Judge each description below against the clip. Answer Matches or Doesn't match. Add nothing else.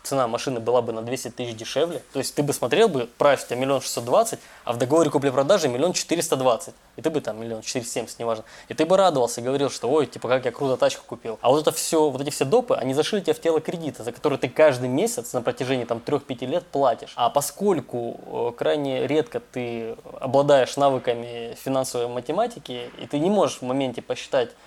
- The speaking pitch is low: Matches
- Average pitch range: Matches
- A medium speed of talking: Doesn't match